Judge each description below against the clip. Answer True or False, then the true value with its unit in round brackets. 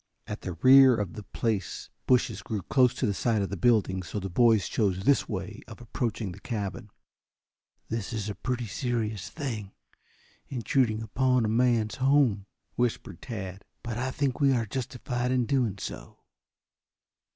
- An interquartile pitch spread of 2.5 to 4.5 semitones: True (3.7 semitones)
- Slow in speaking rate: False (160 wpm)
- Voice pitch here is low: True (115 Hz)